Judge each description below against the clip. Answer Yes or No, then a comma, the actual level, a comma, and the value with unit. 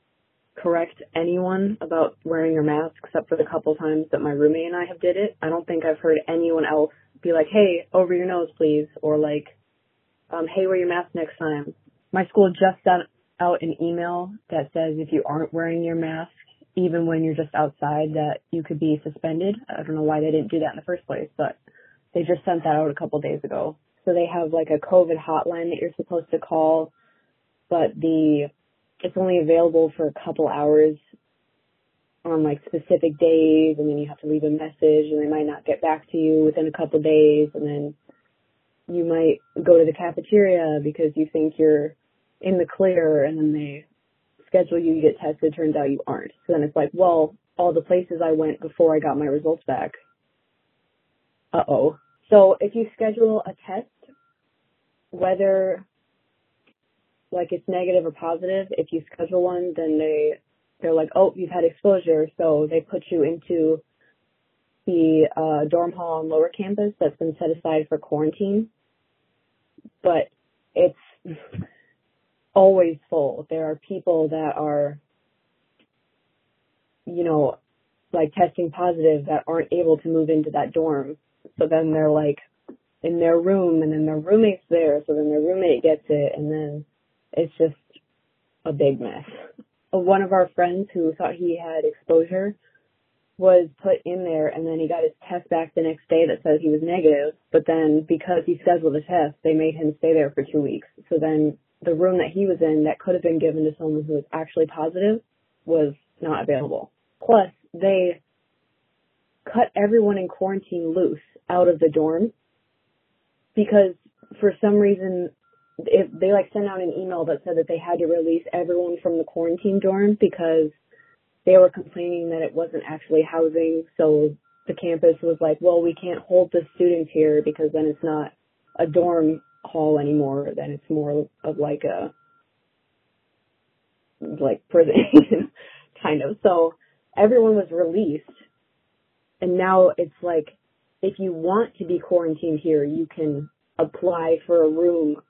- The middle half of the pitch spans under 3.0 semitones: Yes, narrow, 2.5 semitones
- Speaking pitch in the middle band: Yes, medium, 165 Hz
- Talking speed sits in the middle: Yes, average, 175 wpm